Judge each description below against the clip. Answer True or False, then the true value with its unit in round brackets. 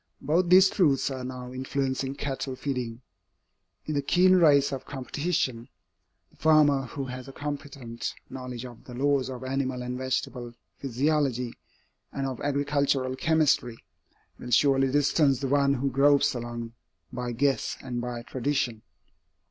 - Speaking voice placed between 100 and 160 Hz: True (135 Hz)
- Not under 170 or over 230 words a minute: False (140 wpm)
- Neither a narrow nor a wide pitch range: False (2.2 semitones)